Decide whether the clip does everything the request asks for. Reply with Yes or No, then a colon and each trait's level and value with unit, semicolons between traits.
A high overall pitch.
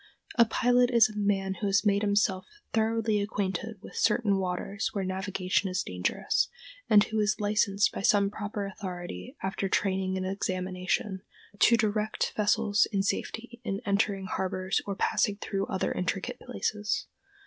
Yes: high, 200 Hz